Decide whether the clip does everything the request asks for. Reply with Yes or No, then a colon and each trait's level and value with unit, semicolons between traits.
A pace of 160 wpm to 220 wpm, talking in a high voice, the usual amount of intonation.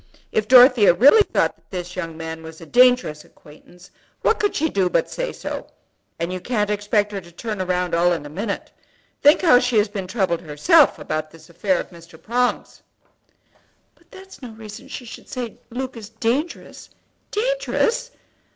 No: average, 180 wpm; high, 210 Hz; wide, 6.3 semitones